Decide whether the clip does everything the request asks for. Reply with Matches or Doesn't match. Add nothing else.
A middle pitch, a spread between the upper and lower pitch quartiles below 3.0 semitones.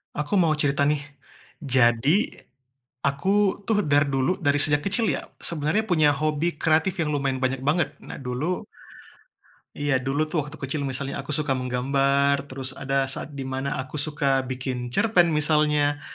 Matches